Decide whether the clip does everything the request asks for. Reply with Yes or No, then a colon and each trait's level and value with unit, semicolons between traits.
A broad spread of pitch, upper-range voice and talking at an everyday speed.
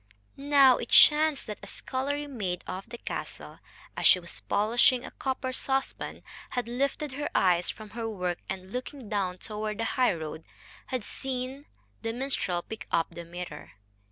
Yes: wide, 6.1 semitones; high, 230 Hz; average, 160 wpm